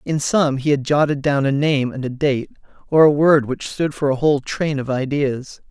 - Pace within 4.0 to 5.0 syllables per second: Yes, 4.8 syllables/s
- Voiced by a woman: No, male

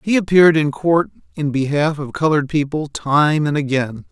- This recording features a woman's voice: No, male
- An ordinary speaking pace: Yes, average, 175 wpm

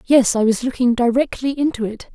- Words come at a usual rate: Yes, average, 195 wpm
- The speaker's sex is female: Yes, female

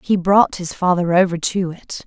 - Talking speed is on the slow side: No, fast, 205 wpm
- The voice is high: No, medium, 180 Hz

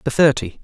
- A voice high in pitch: No, low, 130 Hz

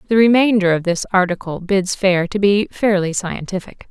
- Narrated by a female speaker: Yes, female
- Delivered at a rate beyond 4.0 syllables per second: Yes, 5.0 syllables/s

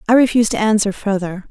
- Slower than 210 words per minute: Yes, average, 200 wpm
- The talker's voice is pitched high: Yes, high, 210 Hz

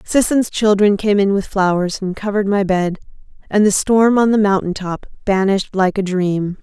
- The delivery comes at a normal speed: Yes, average, 180 wpm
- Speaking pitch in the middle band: No, high, 200 Hz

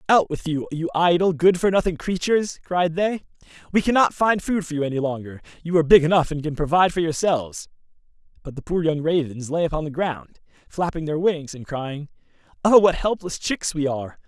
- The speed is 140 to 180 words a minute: No, average, 200 wpm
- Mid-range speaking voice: Yes, medium, 165 Hz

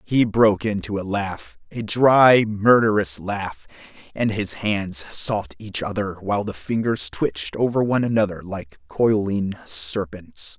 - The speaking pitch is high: No, low, 105 Hz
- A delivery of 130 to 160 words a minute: Yes, average, 140 wpm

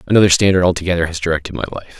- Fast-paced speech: Yes, fast, 210 wpm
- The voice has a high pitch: No, very low, 90 Hz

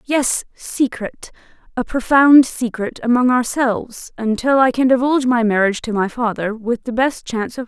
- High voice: Yes, high, 245 Hz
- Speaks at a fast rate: No, average, 155 wpm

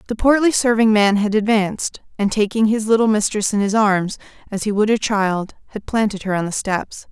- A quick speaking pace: Yes, fast, 210 wpm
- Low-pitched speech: No, high, 210 Hz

